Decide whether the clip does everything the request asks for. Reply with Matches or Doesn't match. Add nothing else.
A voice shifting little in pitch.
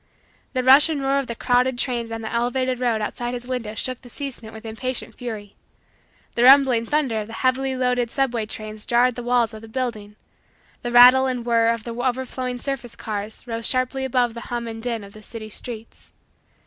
Matches